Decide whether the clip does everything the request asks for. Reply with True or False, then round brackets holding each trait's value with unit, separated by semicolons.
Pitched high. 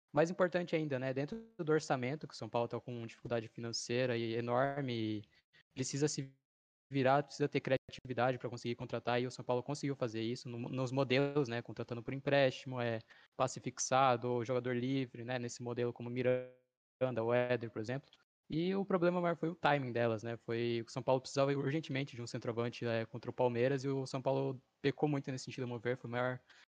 False (125 Hz)